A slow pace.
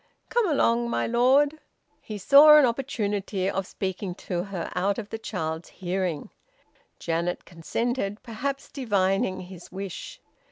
Yes: slow, 130 wpm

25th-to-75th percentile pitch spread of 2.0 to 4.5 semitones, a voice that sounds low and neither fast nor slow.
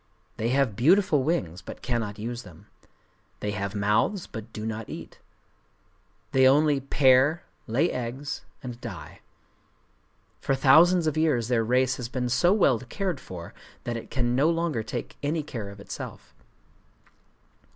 No: average, 5.0 semitones; low, 125 Hz; average, 150 wpm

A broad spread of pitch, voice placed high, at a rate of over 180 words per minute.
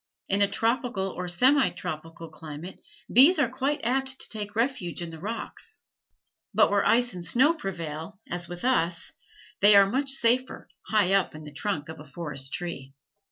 No: wide, 6.8 semitones; high, 195 Hz; average, 175 wpm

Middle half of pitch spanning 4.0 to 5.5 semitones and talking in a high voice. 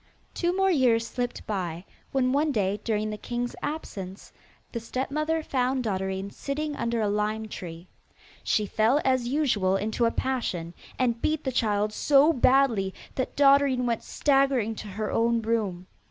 Yes: average, 4.5 semitones; high, 235 Hz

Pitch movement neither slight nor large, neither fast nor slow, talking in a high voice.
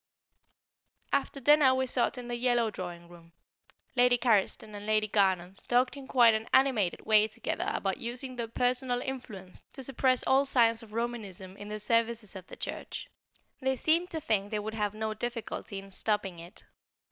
Yes: average, 3.6 semitones; average, 175 wpm; high, 230 Hz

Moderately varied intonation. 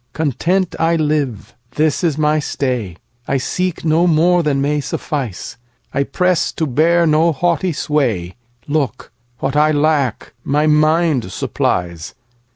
Yes: average, 4.2 semitones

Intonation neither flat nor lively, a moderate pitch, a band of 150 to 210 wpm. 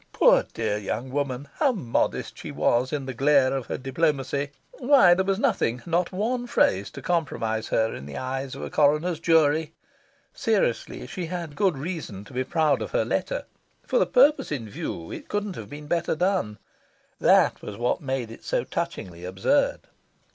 No: wide, 6.5 semitones; medium, 145 Hz; average, 180 wpm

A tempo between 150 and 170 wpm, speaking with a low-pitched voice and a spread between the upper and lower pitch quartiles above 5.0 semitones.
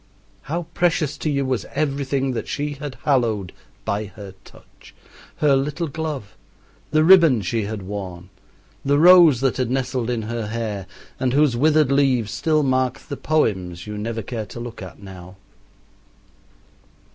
Yes: average, 155 wpm; low, 130 Hz; wide, 5.5 semitones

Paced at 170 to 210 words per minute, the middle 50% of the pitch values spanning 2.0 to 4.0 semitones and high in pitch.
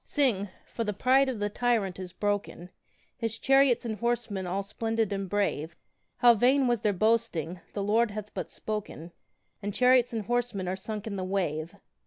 Yes: average, 180 wpm; average, 3.6 semitones; high, 210 Hz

